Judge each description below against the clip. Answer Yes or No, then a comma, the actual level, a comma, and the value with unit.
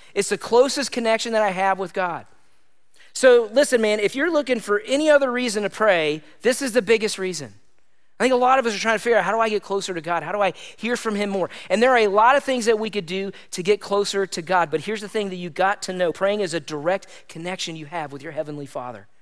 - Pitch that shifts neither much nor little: Yes, average, 4.4 semitones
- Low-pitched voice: No, high, 205 Hz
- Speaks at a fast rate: Yes, fast, 270 wpm